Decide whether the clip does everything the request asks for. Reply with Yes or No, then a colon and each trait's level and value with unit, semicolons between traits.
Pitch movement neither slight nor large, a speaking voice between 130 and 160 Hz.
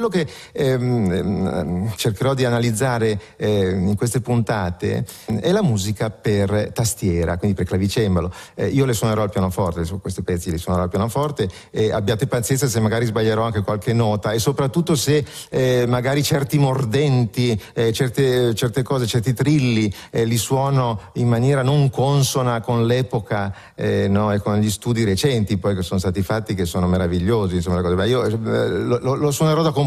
No: average, 4.6 semitones; low, 115 Hz